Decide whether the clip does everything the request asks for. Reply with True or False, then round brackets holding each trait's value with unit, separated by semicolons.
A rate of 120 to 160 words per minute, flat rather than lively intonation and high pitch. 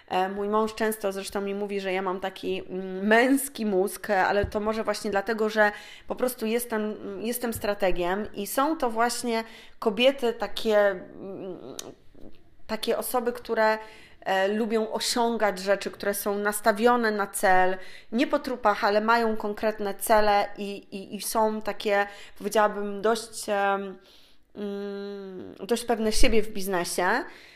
True (130 wpm; 2.2 semitones; 210 Hz)